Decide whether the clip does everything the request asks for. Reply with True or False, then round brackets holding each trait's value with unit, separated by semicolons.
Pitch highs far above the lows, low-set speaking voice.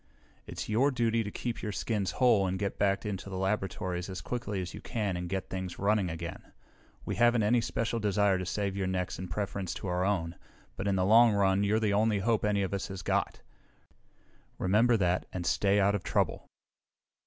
False (2.5 semitones; 100 Hz)